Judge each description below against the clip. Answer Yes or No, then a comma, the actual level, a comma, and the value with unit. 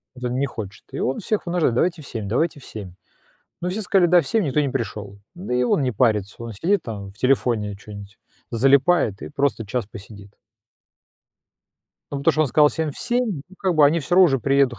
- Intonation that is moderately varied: No, wide, 6.9 semitones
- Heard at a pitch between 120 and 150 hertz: Yes, low, 135 Hz